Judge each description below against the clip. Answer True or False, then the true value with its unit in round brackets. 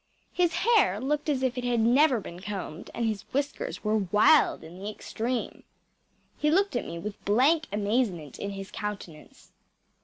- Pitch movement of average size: False (6.0 semitones)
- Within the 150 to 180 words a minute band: True (165 wpm)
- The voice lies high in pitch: True (225 Hz)